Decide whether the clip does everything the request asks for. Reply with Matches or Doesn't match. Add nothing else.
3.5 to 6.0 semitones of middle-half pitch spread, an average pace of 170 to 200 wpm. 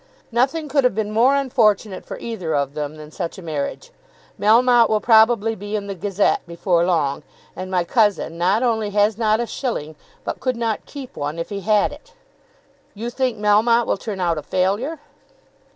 Matches